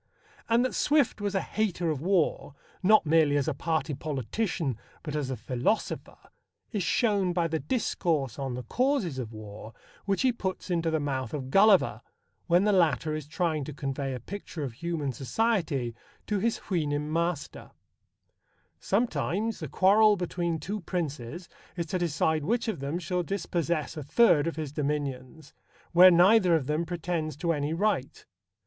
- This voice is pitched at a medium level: Yes, medium, 165 Hz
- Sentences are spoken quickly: No, average, 165 wpm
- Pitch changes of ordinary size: Yes, average, 4.9 semitones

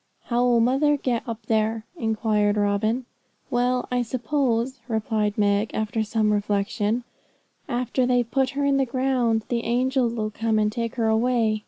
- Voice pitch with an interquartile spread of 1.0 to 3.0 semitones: Yes, narrow, 2.5 semitones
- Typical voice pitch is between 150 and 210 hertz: No, high, 230 Hz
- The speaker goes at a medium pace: Yes, average, 160 wpm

